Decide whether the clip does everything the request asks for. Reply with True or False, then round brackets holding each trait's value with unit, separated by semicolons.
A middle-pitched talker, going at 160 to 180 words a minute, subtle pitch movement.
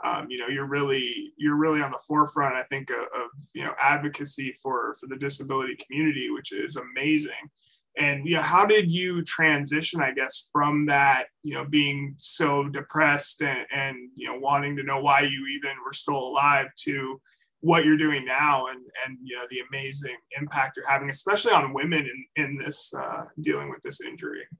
False (145 Hz; 195 wpm; 2.2 semitones)